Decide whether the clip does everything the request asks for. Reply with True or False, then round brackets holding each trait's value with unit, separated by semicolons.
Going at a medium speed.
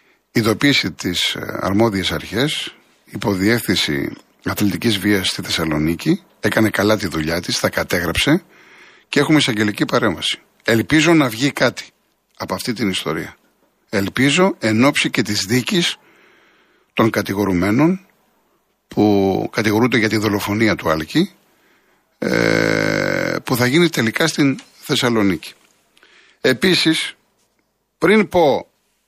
False (105 wpm)